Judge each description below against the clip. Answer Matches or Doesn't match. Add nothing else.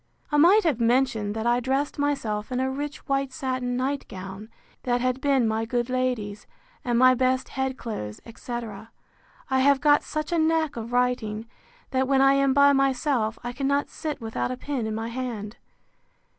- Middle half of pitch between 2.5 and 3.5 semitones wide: Matches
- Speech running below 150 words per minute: Doesn't match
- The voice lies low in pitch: Doesn't match